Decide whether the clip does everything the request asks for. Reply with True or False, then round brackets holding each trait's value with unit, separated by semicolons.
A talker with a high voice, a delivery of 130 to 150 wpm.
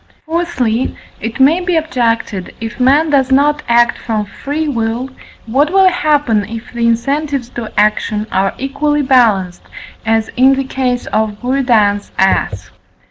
True (250 Hz; 140 wpm)